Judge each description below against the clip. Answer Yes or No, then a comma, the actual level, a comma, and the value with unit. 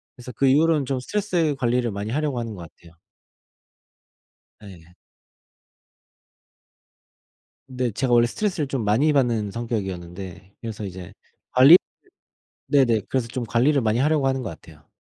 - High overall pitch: No, low, 120 Hz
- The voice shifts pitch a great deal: No, average, 4.8 semitones